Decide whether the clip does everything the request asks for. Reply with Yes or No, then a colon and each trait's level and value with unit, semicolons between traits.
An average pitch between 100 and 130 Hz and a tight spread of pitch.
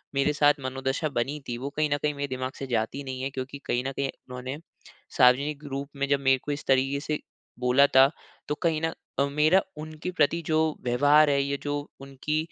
No: medium, 140 Hz; narrow, 2.0 semitones